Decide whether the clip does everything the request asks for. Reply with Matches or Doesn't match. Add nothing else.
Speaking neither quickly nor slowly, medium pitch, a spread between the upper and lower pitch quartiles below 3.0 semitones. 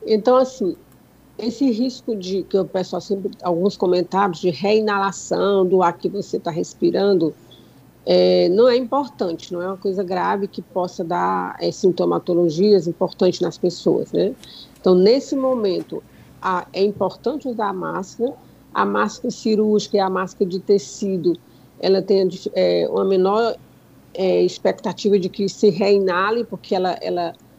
Doesn't match